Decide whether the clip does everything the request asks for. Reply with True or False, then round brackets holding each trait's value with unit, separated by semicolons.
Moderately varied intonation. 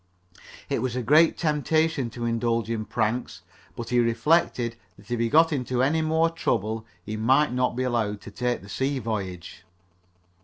True (4.4 semitones)